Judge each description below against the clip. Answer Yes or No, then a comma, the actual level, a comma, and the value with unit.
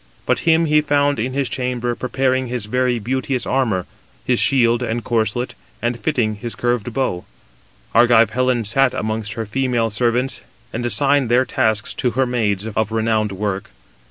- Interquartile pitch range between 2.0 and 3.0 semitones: Yes, average, 2.7 semitones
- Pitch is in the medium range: No, low, 120 Hz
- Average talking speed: Yes, average, 160 wpm